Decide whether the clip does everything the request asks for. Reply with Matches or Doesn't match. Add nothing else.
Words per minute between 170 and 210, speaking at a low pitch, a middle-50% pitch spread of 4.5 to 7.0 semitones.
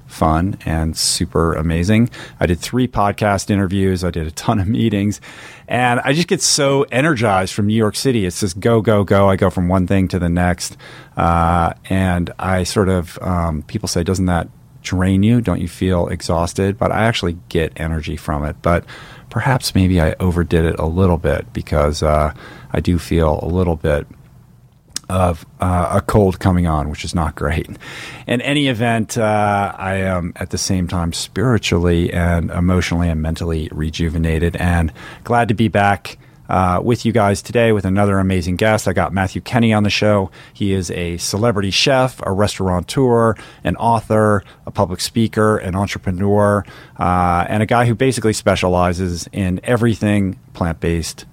Doesn't match